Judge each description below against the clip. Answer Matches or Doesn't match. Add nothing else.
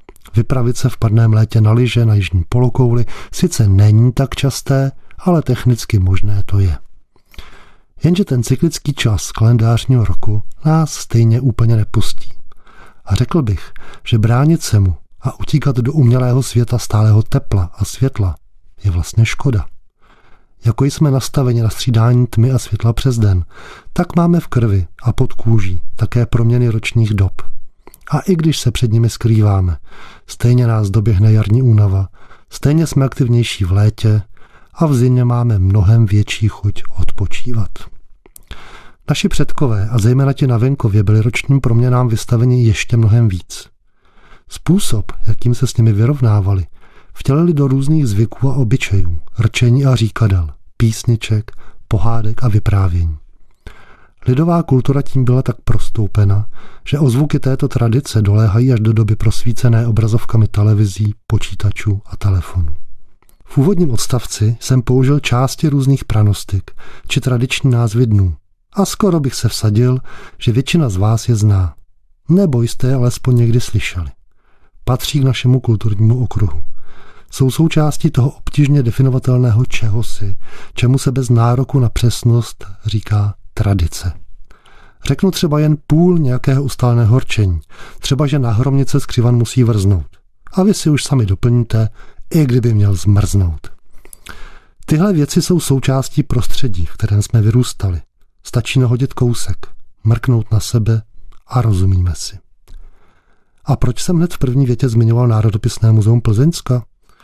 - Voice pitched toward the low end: Matches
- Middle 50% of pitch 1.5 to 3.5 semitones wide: Doesn't match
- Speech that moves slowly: Doesn't match